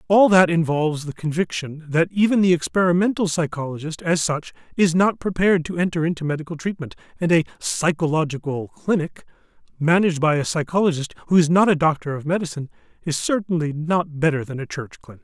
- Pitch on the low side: No, medium, 165 Hz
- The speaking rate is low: No, average, 170 wpm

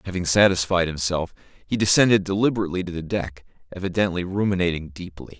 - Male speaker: Yes, male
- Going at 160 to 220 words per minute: No, slow, 135 wpm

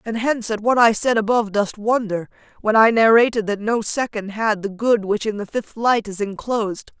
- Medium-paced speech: No, fast, 215 wpm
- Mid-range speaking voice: No, high, 220 Hz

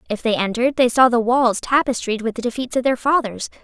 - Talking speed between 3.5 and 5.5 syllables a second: No, 6.0 syllables/s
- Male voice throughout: No, female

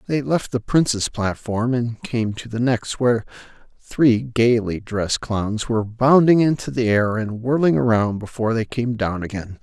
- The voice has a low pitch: Yes, low, 115 Hz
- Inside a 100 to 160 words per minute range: No, average, 175 wpm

